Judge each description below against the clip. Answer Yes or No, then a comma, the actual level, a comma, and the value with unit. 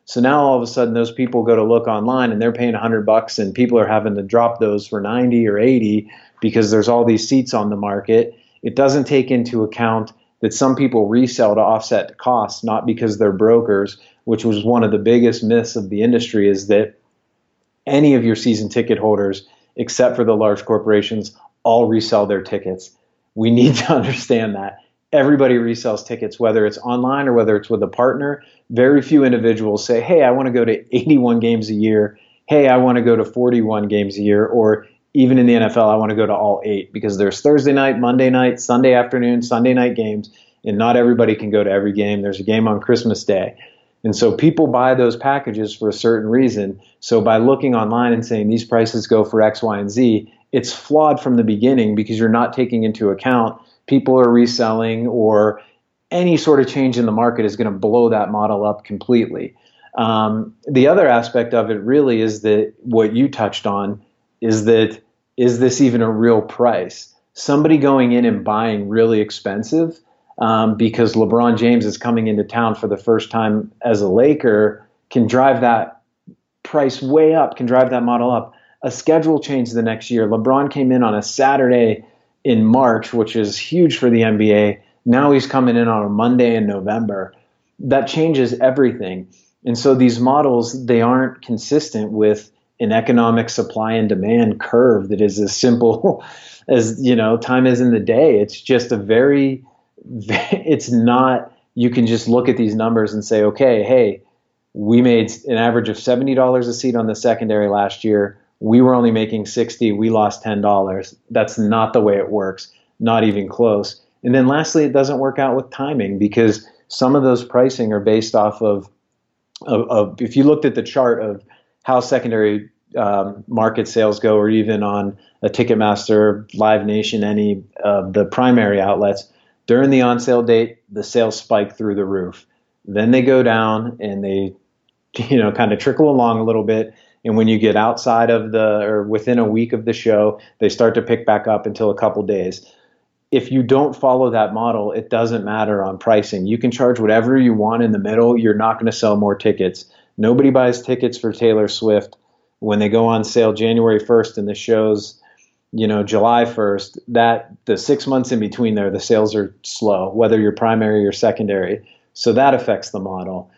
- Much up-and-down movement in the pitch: No, narrow, 2.6 semitones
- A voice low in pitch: Yes, low, 115 Hz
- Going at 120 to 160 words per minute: No, average, 195 wpm